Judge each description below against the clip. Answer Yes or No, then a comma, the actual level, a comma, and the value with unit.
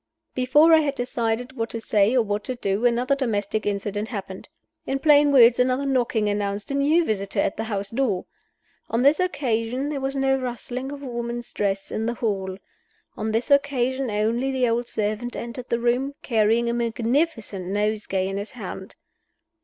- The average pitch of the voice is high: Yes, high, 235 Hz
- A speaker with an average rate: Yes, average, 180 wpm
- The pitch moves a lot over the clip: No, average, 4.0 semitones